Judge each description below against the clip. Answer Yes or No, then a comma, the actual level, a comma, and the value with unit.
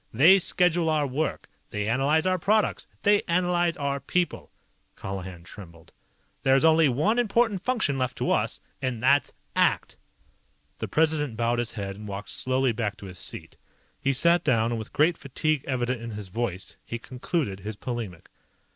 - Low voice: Yes, low, 130 Hz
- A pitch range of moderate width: No, wide, 6.7 semitones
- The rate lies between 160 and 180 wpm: Yes, average, 165 wpm